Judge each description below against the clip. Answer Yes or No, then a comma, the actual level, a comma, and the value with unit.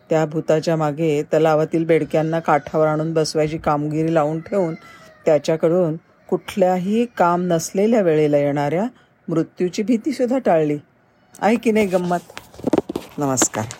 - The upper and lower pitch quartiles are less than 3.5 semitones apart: Yes, average, 3.1 semitones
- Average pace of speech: Yes, average, 105 wpm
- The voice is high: No, medium, 165 Hz